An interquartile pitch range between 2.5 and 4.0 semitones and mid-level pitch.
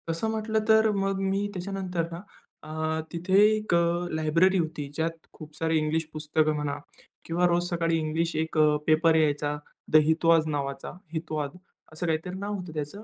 Yes: average, 2.9 semitones; medium, 165 Hz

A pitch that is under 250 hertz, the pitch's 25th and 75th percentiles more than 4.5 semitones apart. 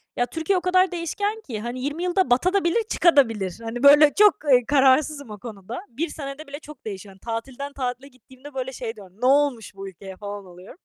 No: very high, 260 Hz; average, 5.2 semitones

